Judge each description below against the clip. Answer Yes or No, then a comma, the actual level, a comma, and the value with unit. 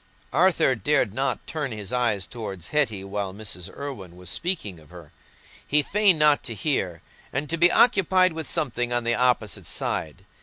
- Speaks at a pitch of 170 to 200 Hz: No, low, 125 Hz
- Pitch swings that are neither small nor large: No, wide, 7.3 semitones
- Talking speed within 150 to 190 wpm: Yes, average, 175 wpm